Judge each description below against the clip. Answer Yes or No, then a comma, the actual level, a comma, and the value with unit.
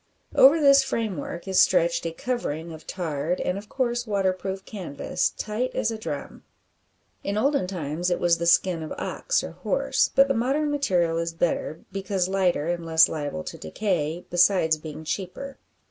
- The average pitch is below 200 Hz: Yes, medium, 185 Hz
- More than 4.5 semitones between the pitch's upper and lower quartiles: Yes, average, 5.0 semitones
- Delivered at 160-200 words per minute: Yes, average, 170 wpm